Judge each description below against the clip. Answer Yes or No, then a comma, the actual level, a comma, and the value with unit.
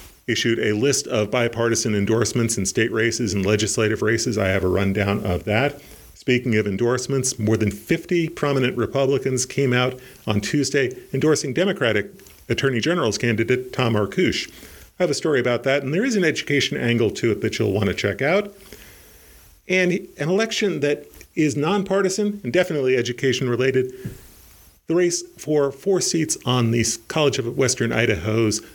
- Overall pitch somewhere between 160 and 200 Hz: No, low, 125 Hz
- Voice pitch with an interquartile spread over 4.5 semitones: Yes, average, 4.9 semitones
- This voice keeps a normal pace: Yes, average, 165 wpm